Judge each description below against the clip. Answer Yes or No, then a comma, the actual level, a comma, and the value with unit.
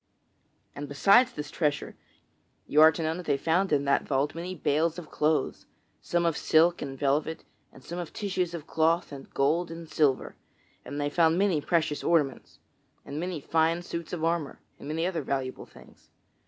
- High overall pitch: No, medium, 160 Hz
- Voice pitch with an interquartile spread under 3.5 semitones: Yes, average, 2.9 semitones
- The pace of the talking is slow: No, average, 180 wpm